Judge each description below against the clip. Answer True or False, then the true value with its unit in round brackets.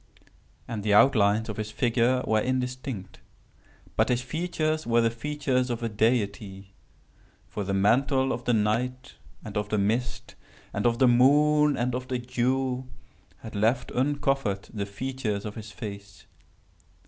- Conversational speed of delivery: True (150 wpm)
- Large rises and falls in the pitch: False (3.6 semitones)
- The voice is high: False (120 Hz)